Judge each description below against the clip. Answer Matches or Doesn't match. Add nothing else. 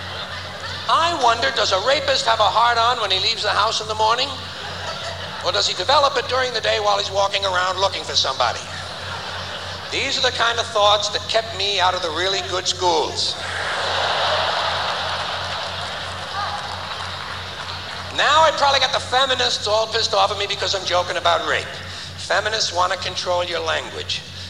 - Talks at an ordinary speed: Matches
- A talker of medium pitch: Doesn't match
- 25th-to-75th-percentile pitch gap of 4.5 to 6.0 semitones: Doesn't match